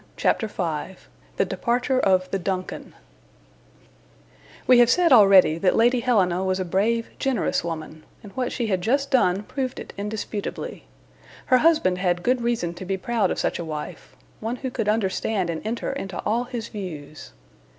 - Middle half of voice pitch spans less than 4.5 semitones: No, average, 4.8 semitones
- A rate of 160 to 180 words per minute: Yes, average, 170 wpm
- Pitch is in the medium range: No, high, 205 Hz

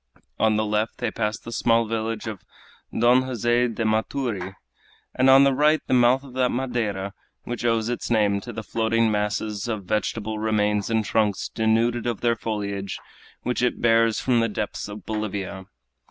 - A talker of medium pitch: No, low, 110 Hz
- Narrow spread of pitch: Yes, narrow, 2.2 semitones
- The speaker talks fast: No, average, 175 wpm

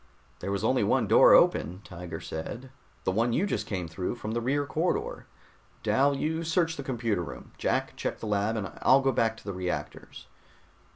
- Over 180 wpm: Yes, average, 190 wpm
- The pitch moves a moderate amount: No, wide, 5.9 semitones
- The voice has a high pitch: No, low, 115 Hz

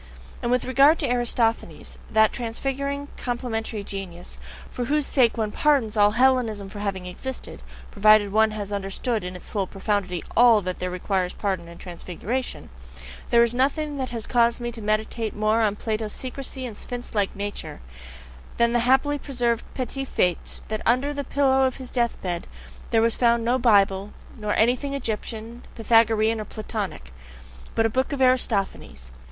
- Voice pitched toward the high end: Yes, high, 225 Hz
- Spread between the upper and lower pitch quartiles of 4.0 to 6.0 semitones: No, average, 3.5 semitones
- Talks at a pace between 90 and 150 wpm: No, average, 165 wpm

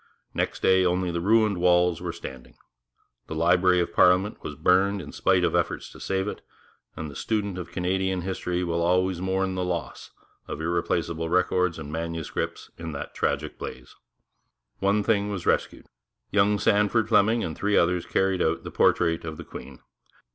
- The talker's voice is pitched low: Yes, very low, 90 Hz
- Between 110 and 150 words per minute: No, average, 170 wpm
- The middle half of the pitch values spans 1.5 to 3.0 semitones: Yes, narrow, 2.4 semitones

